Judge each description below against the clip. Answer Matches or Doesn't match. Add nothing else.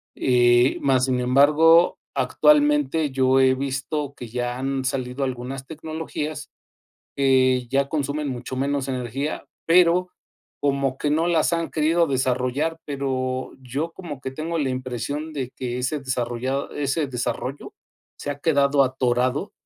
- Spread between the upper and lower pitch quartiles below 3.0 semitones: Matches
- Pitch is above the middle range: Doesn't match